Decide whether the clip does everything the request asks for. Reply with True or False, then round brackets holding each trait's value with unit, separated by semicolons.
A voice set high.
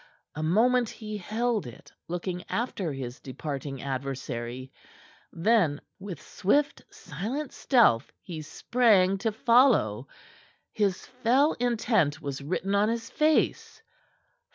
True (195 Hz)